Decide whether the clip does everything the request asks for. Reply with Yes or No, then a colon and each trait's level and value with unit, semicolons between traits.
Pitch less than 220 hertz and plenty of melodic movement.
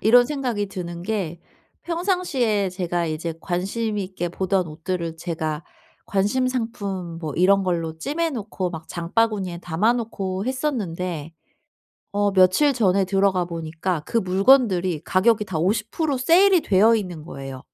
No: high, 190 Hz; average, 4.8 semitones